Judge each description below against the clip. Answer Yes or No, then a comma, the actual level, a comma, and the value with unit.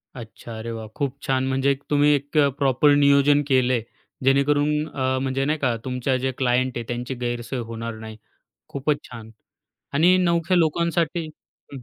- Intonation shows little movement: No, average, 3.0 semitones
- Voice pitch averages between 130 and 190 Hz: Yes, low, 135 Hz